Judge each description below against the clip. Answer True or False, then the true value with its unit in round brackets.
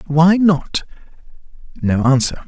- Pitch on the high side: False (155 Hz)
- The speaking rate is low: True (95 wpm)